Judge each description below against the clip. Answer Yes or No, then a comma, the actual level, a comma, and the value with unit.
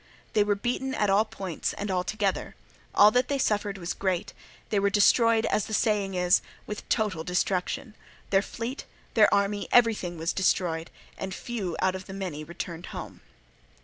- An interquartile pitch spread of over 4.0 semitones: No, average, 2.9 semitones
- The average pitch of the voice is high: Yes, high, 200 Hz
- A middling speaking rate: Yes, average, 170 wpm